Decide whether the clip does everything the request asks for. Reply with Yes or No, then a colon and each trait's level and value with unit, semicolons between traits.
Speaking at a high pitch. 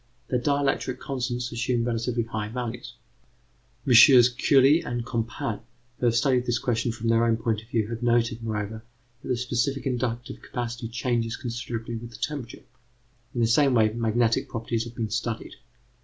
No: low, 120 Hz